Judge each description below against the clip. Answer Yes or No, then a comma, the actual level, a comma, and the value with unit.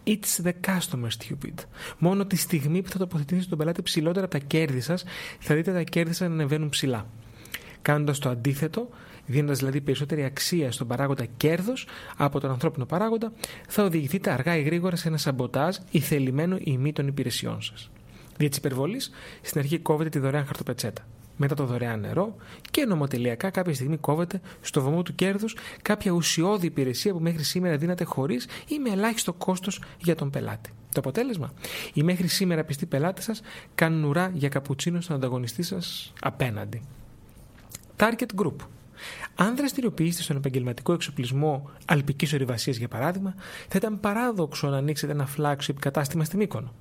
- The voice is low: No, medium, 155 Hz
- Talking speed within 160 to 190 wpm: Yes, average, 165 wpm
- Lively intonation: No, average, 4.7 semitones